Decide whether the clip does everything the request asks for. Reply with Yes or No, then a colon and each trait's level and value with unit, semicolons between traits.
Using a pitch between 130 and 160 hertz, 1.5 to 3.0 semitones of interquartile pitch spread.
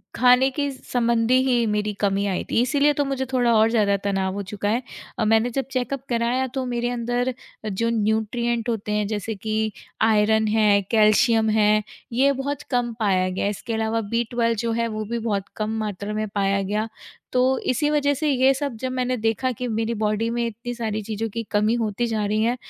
No: high, 225 Hz; average, 2.7 semitones